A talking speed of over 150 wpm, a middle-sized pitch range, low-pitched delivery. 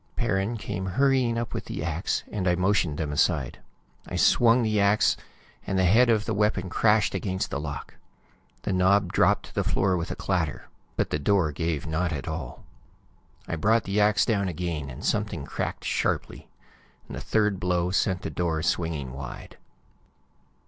Yes: average, 175 wpm; average, 4.3 semitones; very low, 95 Hz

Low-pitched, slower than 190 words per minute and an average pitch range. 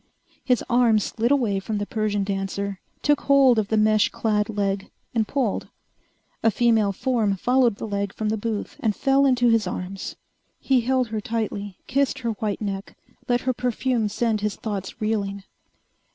No: high, 220 Hz; average, 170 wpm; average, 3.3 semitones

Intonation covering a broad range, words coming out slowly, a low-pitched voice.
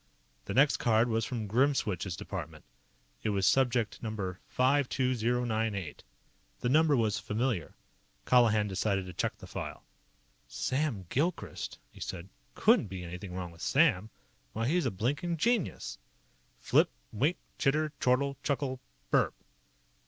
Yes: wide, 5.8 semitones; slow, 125 wpm; low, 115 Hz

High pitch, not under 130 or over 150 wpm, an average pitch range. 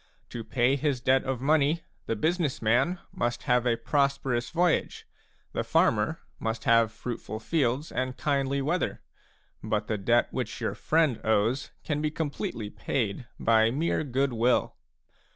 No: low, 130 Hz; average, 145 wpm; average, 4.0 semitones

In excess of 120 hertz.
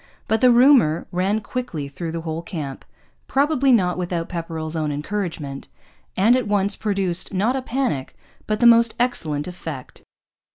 Yes: medium, 185 Hz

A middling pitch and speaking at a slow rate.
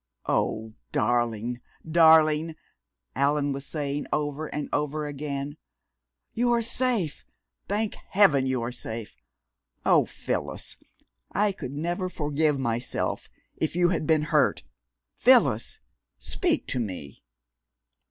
Yes: medium, 150 Hz; slow, 115 wpm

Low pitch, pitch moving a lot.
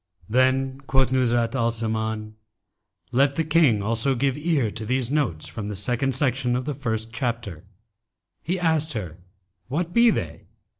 No: low, 125 Hz; average, 3.9 semitones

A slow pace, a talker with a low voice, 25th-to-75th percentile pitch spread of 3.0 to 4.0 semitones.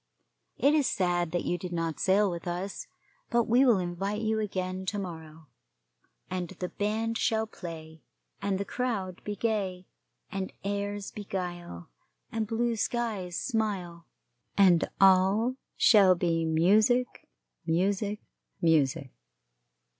No: slow, 125 wpm; high, 195 Hz; average, 3.7 semitones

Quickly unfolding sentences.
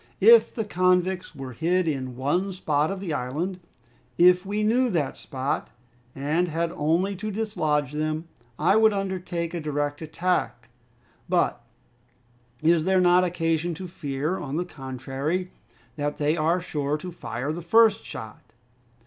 No: average, 150 wpm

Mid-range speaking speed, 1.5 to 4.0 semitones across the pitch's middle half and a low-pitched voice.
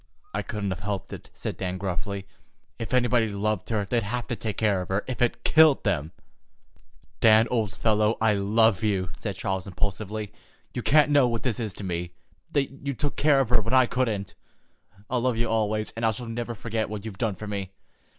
No: fast, 210 wpm; average, 3.2 semitones; low, 110 Hz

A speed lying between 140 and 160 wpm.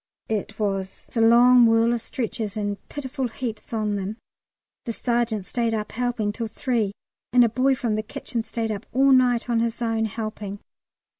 No: average, 175 wpm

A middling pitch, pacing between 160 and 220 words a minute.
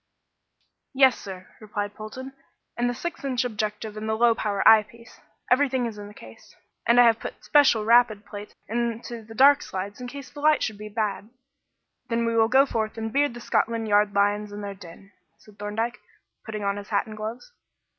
No: high, 220 Hz; average, 200 wpm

